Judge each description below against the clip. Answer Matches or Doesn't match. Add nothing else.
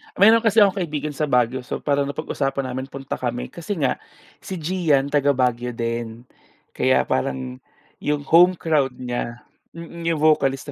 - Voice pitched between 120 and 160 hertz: Matches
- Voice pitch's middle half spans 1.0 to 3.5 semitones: Doesn't match